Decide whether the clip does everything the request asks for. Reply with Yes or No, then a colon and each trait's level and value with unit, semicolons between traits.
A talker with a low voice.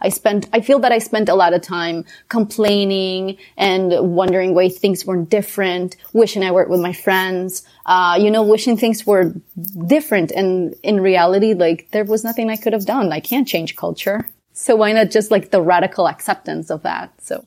No: high, 195 Hz